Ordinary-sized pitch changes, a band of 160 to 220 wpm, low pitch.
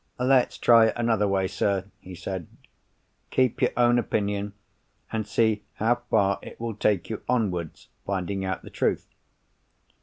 No: average, 3.2 semitones; average, 150 wpm; low, 105 Hz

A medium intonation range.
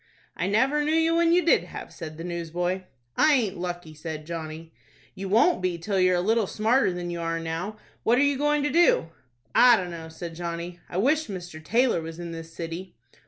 No: wide, 6.1 semitones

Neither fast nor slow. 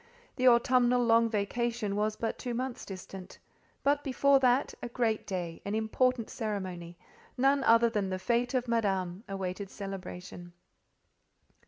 No: slow, 125 wpm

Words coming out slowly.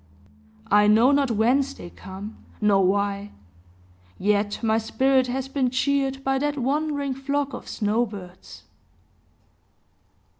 Yes: slow, 120 wpm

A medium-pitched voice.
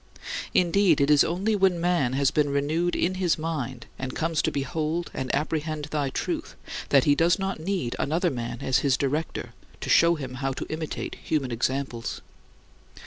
Yes: medium, 150 Hz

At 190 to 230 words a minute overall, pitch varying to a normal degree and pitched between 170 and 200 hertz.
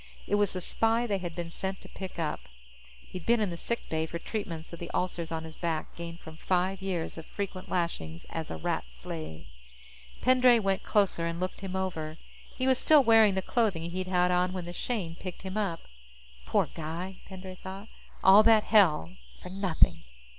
Yes: average, 195 wpm; average, 3.1 semitones; medium, 185 Hz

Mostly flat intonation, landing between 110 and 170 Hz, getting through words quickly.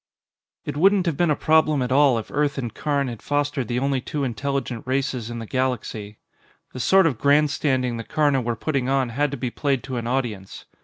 No: average, 3.2 semitones; low, 135 Hz; fast, 210 wpm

